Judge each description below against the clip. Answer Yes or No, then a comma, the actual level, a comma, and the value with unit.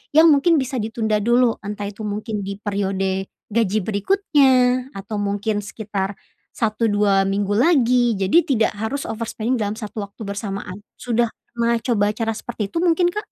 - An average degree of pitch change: Yes, average, 3.4 semitones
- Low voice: No, high, 220 Hz